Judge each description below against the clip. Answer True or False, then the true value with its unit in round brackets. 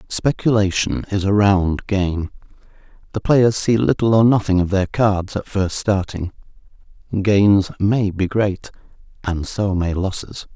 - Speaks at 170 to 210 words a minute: False (135 wpm)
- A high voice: False (100 Hz)